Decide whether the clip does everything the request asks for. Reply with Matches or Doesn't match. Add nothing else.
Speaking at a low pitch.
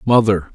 Matches